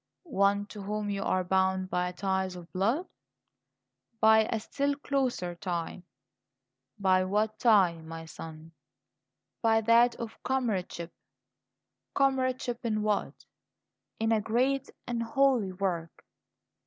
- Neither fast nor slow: No, slow, 115 wpm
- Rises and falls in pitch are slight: No, average, 4.2 semitones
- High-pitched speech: Yes, high, 210 Hz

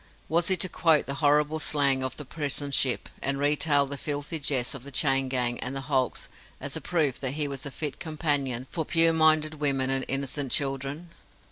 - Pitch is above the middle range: No, medium, 145 Hz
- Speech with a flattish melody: Yes, narrow, 2.3 semitones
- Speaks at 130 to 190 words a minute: No, fast, 205 wpm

